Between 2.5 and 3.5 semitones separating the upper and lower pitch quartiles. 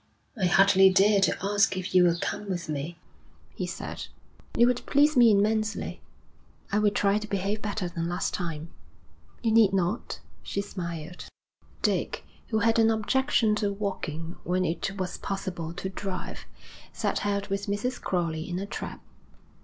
Yes: average, 3.0 semitones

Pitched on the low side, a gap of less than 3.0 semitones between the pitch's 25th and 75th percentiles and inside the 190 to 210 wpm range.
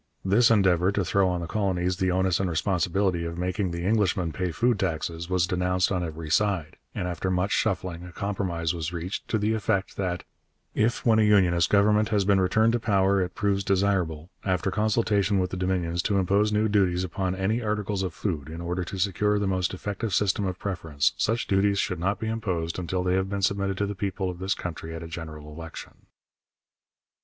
Yes: very low, 95 Hz; narrow, 2.5 semitones; fast, 205 wpm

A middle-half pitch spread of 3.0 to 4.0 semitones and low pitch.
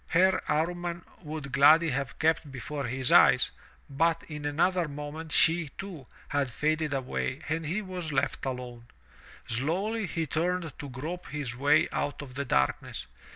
No: average, 3.4 semitones; medium, 150 Hz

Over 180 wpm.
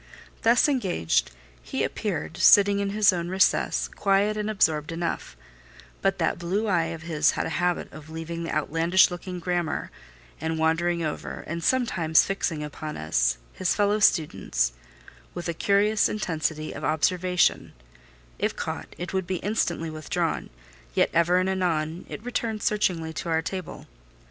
No: average, 155 wpm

